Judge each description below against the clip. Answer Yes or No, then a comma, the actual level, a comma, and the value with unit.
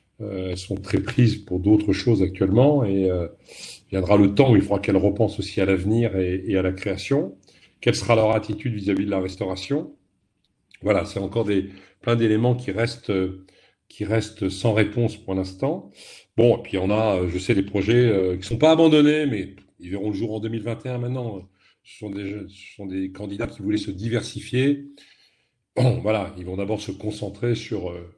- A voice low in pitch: Yes, low, 100 Hz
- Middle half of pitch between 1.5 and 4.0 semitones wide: Yes, average, 3.4 semitones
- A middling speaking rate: Yes, average, 190 wpm